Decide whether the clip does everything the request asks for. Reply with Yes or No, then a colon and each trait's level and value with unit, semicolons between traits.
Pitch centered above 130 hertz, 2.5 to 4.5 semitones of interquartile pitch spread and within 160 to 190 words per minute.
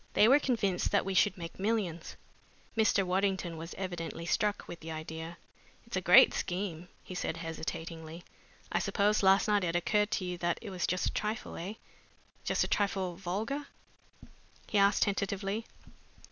Yes: high, 190 Hz; average, 3.2 semitones; average, 165 wpm